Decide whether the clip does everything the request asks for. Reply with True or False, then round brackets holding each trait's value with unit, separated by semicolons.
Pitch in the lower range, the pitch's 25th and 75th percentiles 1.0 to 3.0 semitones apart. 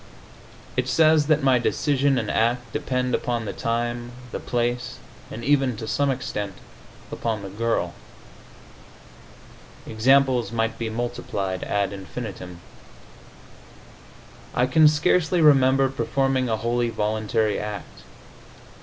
False (120 Hz; 3.4 semitones)